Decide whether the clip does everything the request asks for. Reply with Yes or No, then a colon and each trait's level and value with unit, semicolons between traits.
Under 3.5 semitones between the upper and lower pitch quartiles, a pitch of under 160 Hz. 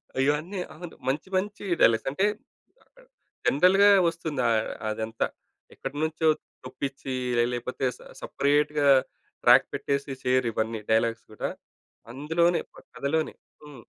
No: average, 4.2 semitones; medium, 140 Hz